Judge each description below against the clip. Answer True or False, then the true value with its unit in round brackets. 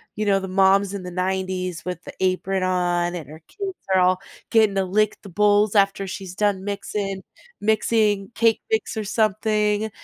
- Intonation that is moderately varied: False (2.2 semitones)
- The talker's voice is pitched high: True (195 Hz)